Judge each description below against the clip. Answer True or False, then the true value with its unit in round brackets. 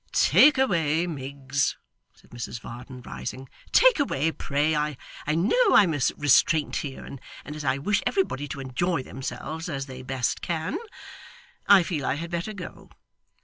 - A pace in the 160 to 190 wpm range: False (150 wpm)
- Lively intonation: False (4.3 semitones)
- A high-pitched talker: False (150 Hz)